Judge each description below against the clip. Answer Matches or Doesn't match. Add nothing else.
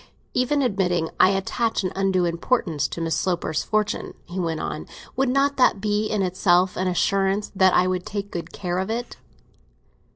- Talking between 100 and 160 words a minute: Doesn't match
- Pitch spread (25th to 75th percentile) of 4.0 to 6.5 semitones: Doesn't match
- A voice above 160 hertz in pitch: Matches